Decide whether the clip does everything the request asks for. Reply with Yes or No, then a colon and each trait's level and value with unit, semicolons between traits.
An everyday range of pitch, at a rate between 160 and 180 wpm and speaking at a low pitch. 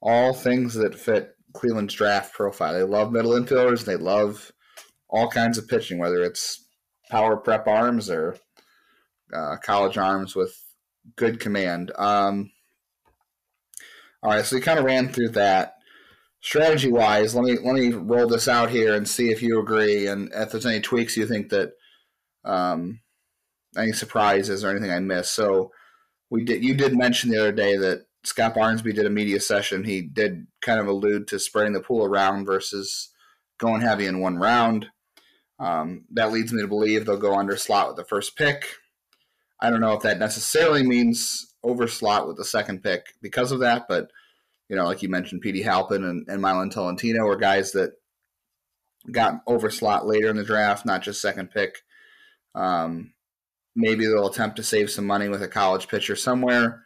Yes: average, 3.2 semitones; average, 175 wpm; low, 110 Hz